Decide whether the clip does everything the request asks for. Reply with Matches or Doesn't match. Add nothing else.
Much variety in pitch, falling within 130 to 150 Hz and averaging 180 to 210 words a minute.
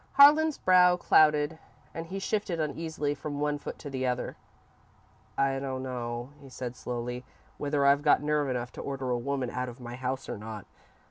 Doesn't match